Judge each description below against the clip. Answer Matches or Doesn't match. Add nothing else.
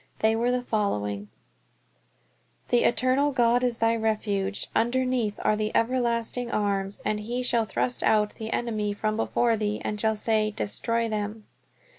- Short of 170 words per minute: Matches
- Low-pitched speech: Doesn't match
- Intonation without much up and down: Matches